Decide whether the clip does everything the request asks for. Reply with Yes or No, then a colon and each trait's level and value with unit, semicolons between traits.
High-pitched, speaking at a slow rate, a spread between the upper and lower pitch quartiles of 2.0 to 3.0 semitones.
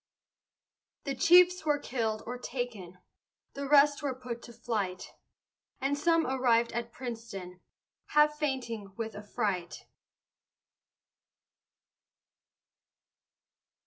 No: high, 245 Hz; slow, 90 wpm; average, 4.4 semitones